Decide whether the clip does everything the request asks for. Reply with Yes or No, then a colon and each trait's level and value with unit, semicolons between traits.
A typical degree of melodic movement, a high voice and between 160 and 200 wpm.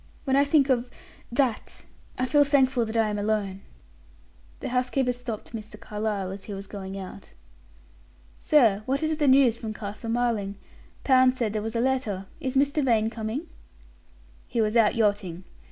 Yes: average, 3.8 semitones; high, 230 Hz; average, 170 wpm